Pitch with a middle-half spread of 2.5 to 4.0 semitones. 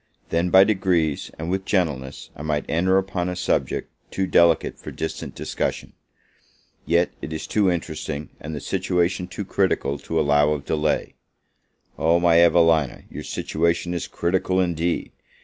Yes: average, 2.8 semitones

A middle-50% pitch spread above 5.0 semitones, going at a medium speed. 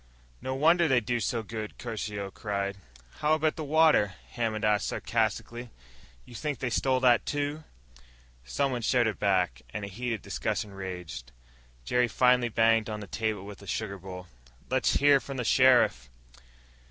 No: average, 4.4 semitones; average, 155 wpm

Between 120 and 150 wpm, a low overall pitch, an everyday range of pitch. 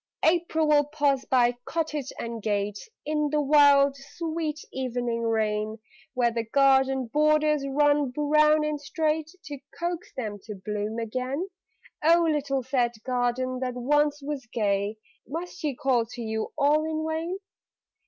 No: average, 145 wpm; very high, 275 Hz; average, 4.2 semitones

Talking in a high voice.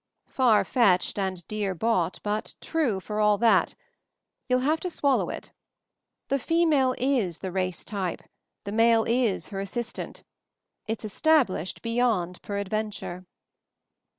Yes: high, 215 Hz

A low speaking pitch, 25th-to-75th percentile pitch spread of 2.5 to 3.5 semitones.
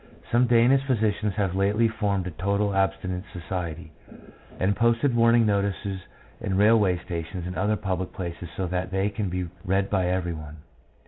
Yes: very low, 95 Hz; average, 2.8 semitones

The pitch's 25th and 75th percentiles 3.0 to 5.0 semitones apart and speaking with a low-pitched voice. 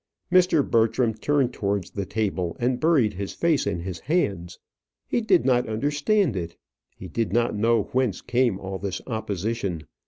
No: wide, 5.4 semitones; low, 115 Hz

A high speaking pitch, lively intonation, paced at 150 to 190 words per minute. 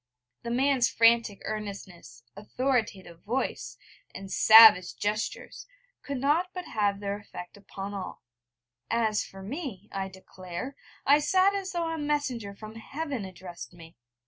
No: high, 215 Hz; wide, 6.0 semitones; slow, 135 wpm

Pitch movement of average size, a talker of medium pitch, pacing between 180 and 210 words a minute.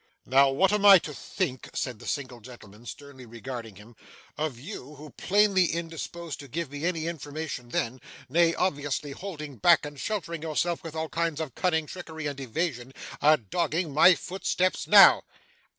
No: average, 4.3 semitones; medium, 150 Hz; average, 165 wpm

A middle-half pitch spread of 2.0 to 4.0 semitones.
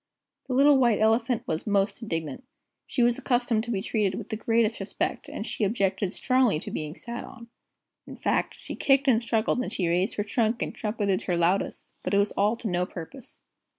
Yes: average, 3.7 semitones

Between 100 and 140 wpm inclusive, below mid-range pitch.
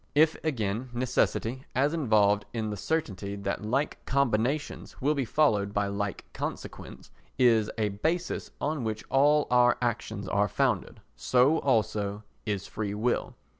Yes: slow, 135 wpm; low, 115 Hz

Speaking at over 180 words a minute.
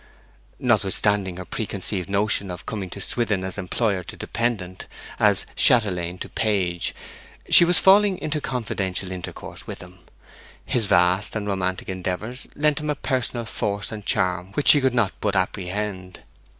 No: average, 150 wpm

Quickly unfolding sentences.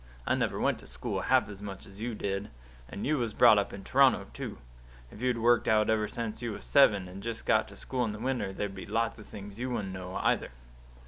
Yes: fast, 245 wpm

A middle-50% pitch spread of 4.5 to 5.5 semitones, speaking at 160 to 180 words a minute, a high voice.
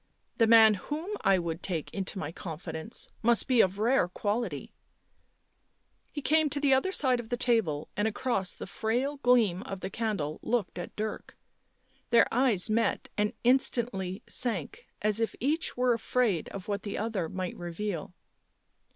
Yes: average, 4.8 semitones; average, 170 wpm; high, 220 Hz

